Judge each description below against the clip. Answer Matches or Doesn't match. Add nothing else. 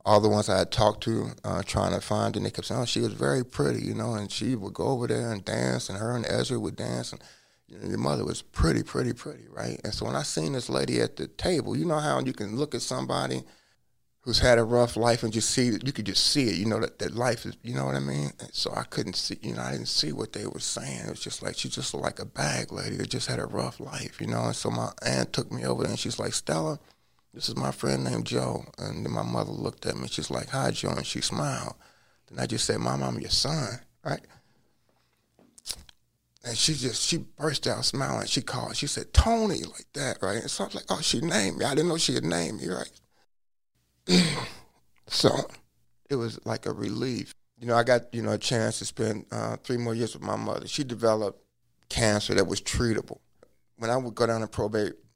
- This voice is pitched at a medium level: Doesn't match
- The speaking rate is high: Matches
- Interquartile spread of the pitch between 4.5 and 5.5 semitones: Matches